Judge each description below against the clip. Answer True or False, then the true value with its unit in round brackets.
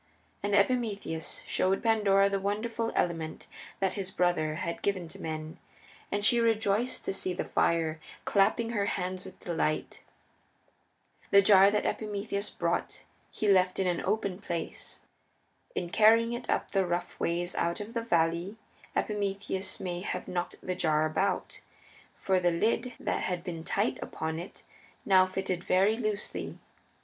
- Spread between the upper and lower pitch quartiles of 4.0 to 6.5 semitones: False (2.9 semitones)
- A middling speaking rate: True (150 wpm)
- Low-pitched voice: False (190 Hz)